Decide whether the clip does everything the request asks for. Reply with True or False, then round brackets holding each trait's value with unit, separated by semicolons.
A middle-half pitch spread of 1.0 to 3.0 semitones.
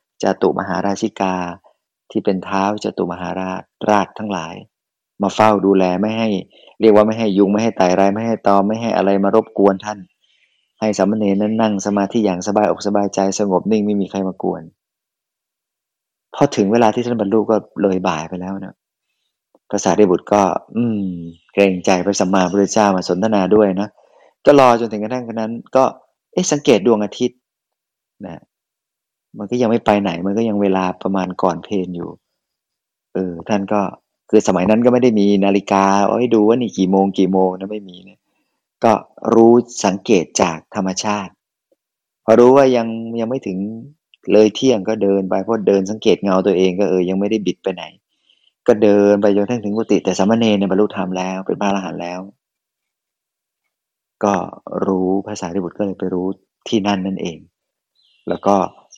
True (2.5 semitones)